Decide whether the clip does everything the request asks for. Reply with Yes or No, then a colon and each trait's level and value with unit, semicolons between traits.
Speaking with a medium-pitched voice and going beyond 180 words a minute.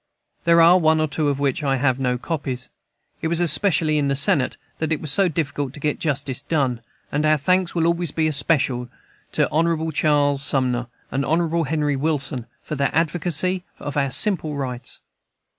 Yes: medium, 150 Hz; average, 190 wpm